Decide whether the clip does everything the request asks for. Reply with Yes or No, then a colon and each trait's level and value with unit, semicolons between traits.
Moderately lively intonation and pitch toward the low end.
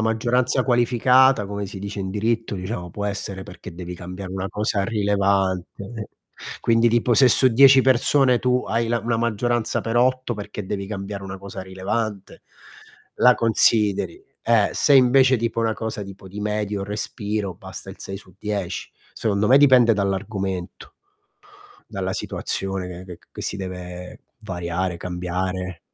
Yes: average, 3.5 semitones; low, 105 Hz